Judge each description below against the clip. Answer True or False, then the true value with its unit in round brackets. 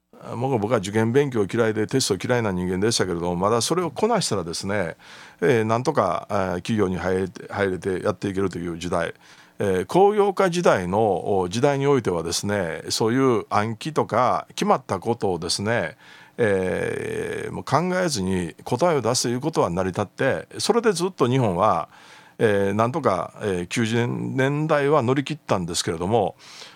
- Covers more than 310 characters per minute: True (335 characters per minute)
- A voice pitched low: True (115 Hz)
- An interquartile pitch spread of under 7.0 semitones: False (7.7 semitones)